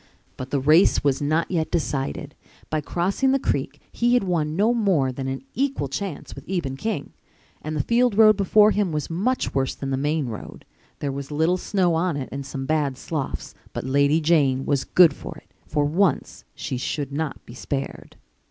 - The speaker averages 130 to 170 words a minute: No, average, 195 wpm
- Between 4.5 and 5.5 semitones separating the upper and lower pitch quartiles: Yes, average, 5.1 semitones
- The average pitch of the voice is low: No, medium, 155 Hz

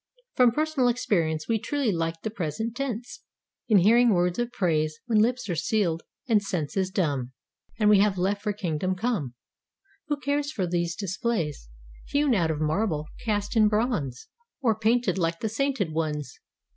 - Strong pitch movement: Yes, wide, 6.1 semitones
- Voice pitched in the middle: No, high, 200 Hz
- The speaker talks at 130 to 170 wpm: Yes, average, 160 wpm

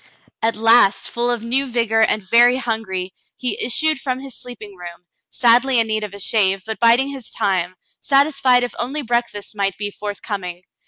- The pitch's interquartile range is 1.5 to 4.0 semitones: Yes, average, 3.5 semitones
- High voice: Yes, high, 230 Hz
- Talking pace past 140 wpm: Yes, average, 180 wpm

